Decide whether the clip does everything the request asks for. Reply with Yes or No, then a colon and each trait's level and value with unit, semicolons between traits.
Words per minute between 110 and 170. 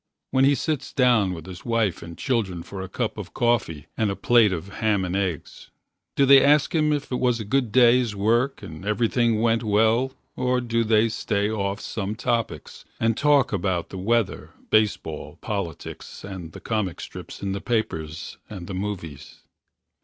No: average, 180 wpm